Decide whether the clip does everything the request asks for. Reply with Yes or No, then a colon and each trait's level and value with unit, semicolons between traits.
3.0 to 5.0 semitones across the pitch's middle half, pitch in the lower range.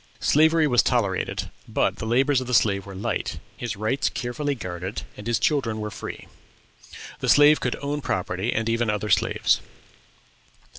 Yes: average, 4.7 semitones; low, 115 Hz